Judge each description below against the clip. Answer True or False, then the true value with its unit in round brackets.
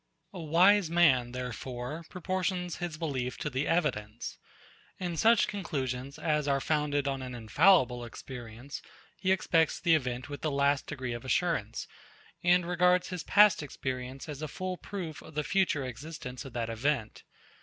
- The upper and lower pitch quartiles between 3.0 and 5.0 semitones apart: False (5.4 semitones)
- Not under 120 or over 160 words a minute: True (155 wpm)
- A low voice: False (150 Hz)